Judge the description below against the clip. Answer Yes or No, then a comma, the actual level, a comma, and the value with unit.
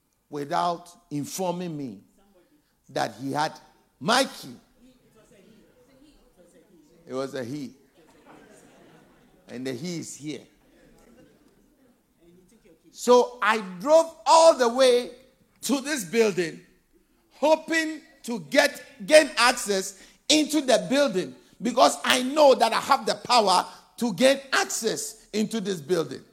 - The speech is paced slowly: Yes, slow, 110 wpm